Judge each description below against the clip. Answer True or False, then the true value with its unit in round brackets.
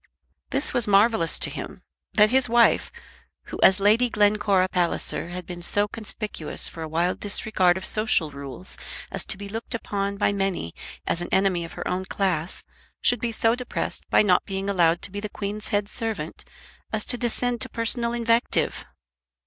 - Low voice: False (205 Hz)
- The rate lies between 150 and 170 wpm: False (180 wpm)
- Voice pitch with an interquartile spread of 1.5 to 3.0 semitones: False (3.7 semitones)